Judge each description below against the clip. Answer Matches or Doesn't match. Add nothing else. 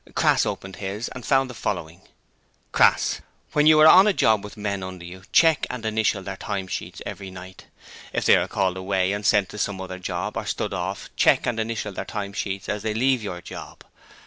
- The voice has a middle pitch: Doesn't match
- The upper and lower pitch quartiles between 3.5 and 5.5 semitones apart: Doesn't match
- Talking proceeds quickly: Matches